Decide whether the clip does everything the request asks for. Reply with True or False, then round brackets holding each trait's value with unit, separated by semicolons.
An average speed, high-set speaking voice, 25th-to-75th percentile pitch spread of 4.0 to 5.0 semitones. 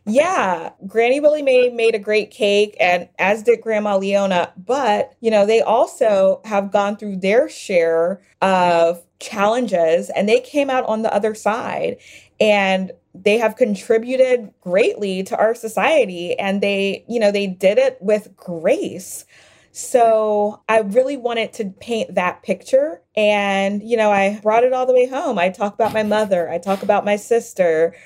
False (165 wpm; 210 Hz; 3.3 semitones)